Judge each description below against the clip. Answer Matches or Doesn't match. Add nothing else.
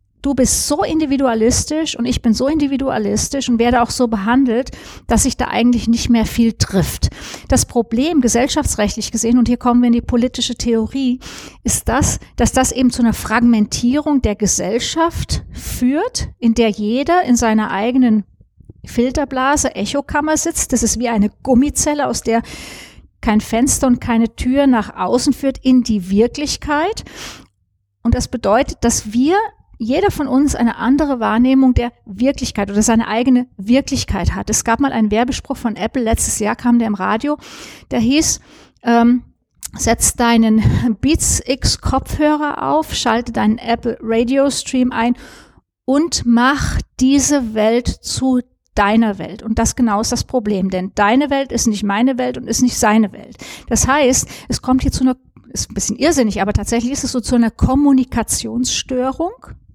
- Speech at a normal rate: Matches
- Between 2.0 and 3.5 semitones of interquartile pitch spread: Matches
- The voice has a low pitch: Doesn't match